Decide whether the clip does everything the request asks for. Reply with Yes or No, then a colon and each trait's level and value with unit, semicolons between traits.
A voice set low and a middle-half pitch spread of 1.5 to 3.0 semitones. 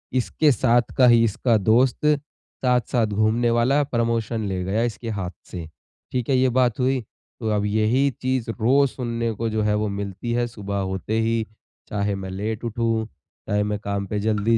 Yes: low, 115 Hz; average, 2.7 semitones